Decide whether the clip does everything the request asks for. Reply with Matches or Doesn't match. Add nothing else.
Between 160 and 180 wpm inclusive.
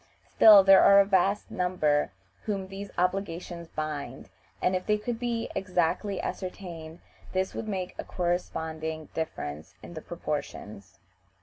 Doesn't match